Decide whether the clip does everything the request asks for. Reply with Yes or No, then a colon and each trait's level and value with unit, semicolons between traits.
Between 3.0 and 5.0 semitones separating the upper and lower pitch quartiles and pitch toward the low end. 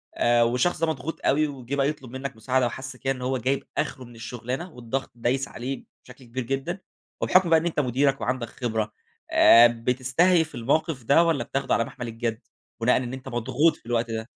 No: narrow, 2.6 semitones; low, 130 Hz